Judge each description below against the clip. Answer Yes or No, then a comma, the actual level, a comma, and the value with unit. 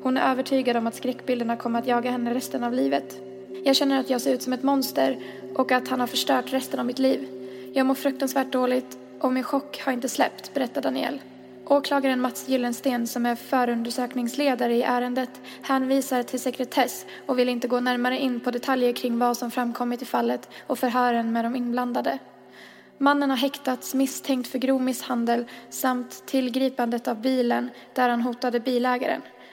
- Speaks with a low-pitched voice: No, very high, 250 Hz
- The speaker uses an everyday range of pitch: No, narrow, 1.6 semitones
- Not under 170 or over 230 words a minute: Yes, average, 180 wpm